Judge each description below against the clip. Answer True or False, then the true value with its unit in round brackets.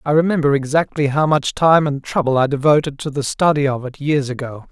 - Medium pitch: True (145 Hz)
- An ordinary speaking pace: False (215 wpm)